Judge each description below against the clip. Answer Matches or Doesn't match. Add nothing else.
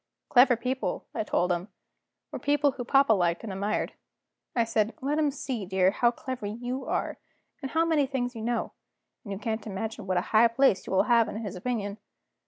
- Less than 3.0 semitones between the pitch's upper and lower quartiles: Doesn't match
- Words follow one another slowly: Doesn't match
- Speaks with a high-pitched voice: Matches